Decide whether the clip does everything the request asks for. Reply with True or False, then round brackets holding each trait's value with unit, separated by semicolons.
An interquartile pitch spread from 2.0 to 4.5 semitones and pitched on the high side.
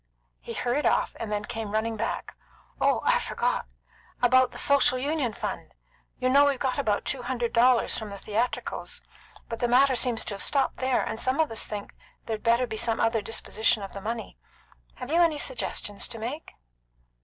True (2.9 semitones; 240 Hz)